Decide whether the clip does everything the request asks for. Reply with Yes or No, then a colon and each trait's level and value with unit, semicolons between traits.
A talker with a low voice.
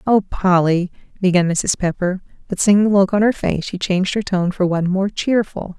No: high, 190 Hz